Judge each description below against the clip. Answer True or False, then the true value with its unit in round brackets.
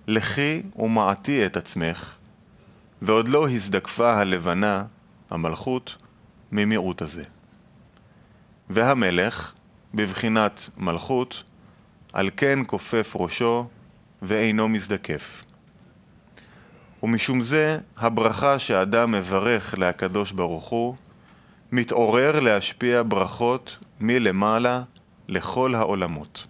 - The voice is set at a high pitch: False (110 Hz)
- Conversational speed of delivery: False (75 wpm)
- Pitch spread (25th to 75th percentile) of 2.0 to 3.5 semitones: False (4.3 semitones)